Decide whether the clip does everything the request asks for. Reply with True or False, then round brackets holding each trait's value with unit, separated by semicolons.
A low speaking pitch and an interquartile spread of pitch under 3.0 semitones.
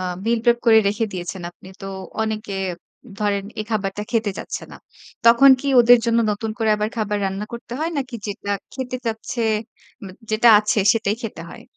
False (220 Hz; 2.4 semitones)